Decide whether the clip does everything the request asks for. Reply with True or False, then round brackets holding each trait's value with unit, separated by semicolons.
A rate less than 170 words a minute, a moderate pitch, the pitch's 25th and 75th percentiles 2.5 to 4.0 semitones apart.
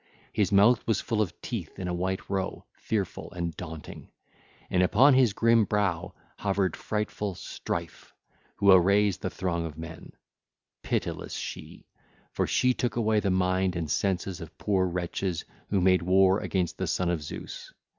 False (160 wpm; 95 Hz; 2.8 semitones)